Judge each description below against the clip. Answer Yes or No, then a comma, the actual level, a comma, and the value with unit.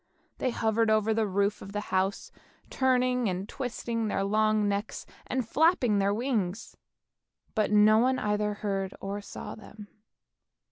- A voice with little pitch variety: Yes, narrow, 2.3 semitones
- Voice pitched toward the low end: No, high, 215 Hz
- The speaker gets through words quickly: No, average, 145 wpm